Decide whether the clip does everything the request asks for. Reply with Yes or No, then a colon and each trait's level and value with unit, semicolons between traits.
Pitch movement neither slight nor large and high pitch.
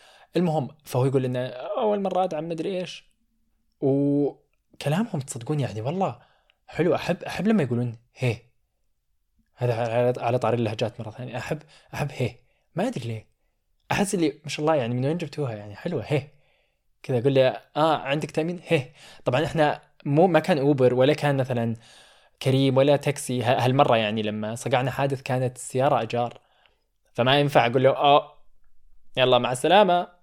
No: average, 4.0 semitones; low, 135 Hz